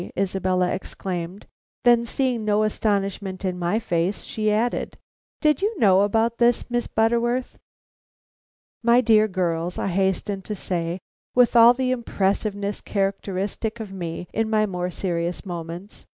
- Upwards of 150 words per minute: No, slow, 135 wpm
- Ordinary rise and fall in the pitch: Yes, average, 3.8 semitones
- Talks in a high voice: Yes, high, 200 Hz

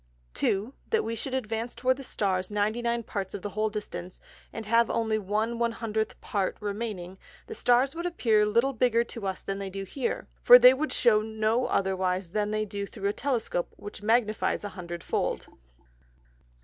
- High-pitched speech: Yes, high, 215 Hz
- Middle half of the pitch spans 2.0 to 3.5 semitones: Yes, average, 2.9 semitones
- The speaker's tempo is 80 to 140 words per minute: No, average, 175 wpm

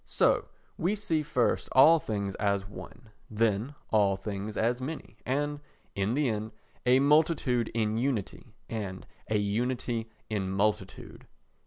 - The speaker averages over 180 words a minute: No, slow, 135 wpm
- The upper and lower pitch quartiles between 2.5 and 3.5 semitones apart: No, average, 4.3 semitones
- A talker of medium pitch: No, low, 115 Hz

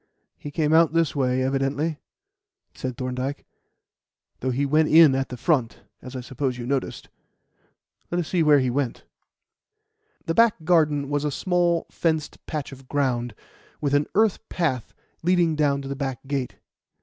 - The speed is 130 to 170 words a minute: Yes, average, 160 wpm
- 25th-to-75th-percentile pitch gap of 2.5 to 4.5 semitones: Yes, average, 3.5 semitones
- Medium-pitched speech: Yes, medium, 145 Hz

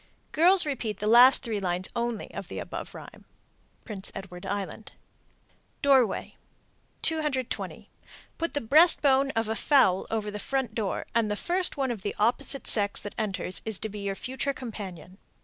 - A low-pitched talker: No, high, 225 Hz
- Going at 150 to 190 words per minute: Yes, average, 170 wpm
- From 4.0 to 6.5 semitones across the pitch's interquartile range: Yes, average, 4.9 semitones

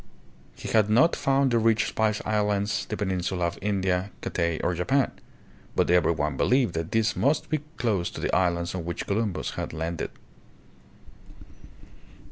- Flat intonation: No, average, 4.5 semitones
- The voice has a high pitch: No, low, 100 Hz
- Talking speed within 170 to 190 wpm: No, average, 160 wpm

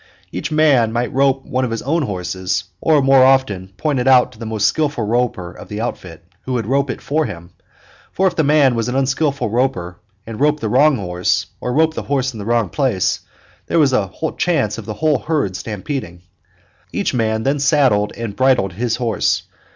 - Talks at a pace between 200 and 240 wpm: Yes, fast, 205 wpm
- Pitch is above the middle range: No, low, 125 Hz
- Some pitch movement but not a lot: Yes, average, 4.9 semitones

